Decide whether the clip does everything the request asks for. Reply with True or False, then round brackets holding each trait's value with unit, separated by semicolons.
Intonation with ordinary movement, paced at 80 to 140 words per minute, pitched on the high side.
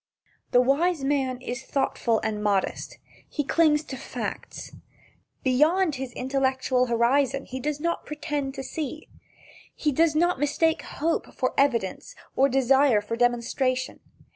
True (3.0 semitones; 135 wpm; 270 Hz)